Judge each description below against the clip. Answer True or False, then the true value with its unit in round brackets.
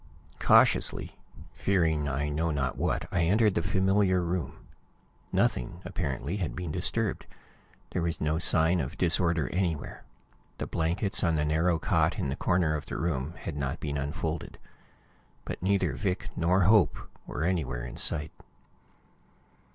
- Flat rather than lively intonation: False (3.8 semitones)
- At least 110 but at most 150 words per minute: True (145 wpm)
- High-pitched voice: False (85 Hz)